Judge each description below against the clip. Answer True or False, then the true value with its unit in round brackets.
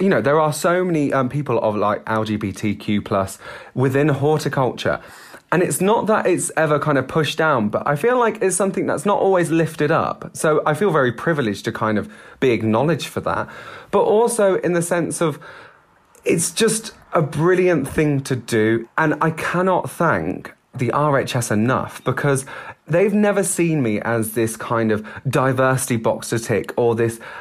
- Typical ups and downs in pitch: False (6.5 semitones)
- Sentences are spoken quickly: False (175 wpm)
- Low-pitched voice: False (145 Hz)